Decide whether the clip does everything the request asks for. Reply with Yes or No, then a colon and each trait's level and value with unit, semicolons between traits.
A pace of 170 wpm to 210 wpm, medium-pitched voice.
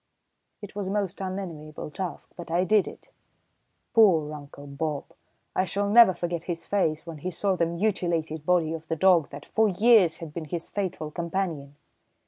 Yes: average, 175 wpm; medium, 170 Hz